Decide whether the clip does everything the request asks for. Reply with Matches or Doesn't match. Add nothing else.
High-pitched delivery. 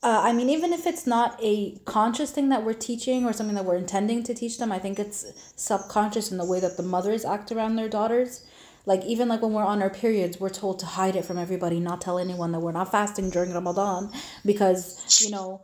Matches